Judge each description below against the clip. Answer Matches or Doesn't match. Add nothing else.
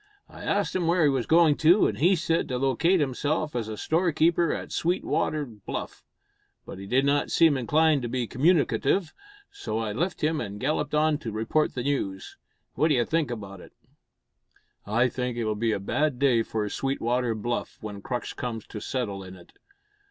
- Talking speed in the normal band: Matches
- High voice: Doesn't match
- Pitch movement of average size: Doesn't match